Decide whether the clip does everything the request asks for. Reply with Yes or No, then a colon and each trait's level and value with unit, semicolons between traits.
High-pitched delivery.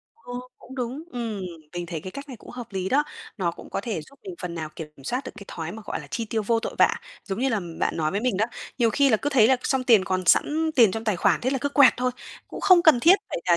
Yes: high, 230 Hz